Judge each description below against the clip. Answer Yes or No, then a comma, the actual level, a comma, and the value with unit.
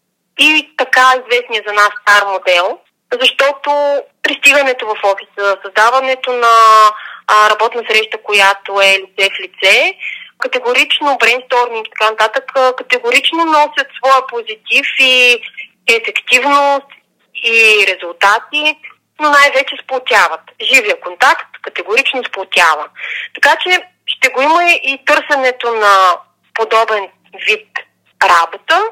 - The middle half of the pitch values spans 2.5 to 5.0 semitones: No, wide, 5.5 semitones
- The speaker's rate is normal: No, slow, 105 wpm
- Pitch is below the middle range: No, very high, 255 Hz